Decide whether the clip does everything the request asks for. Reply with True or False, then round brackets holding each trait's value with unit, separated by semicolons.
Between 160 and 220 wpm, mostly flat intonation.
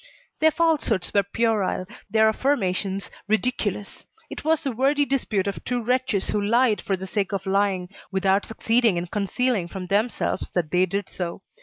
False (165 wpm; 4.3 semitones)